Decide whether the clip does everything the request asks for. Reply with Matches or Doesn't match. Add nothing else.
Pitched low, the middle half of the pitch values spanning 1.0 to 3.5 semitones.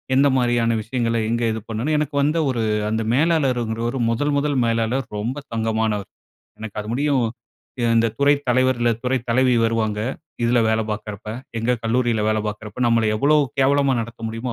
Matches